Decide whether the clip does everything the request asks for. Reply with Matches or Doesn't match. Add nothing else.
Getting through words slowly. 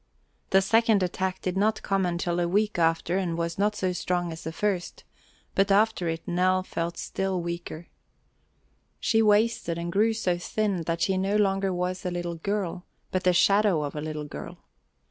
Doesn't match